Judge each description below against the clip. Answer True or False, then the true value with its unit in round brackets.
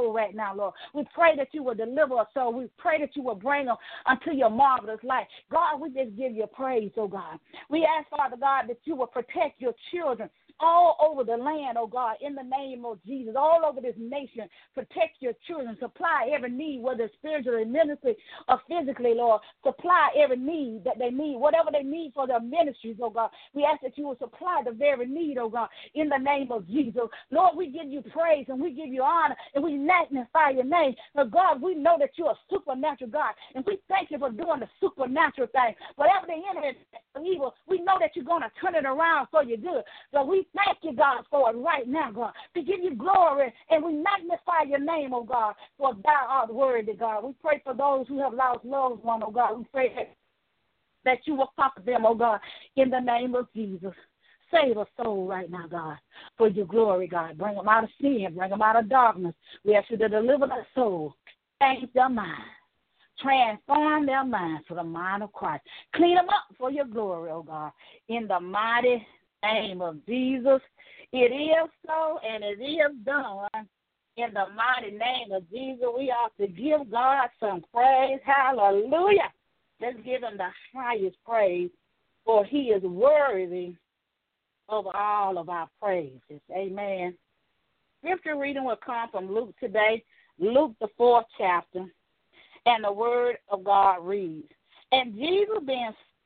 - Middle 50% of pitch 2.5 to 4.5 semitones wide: False (5.2 semitones)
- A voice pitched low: False (260 Hz)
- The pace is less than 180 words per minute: False (195 wpm)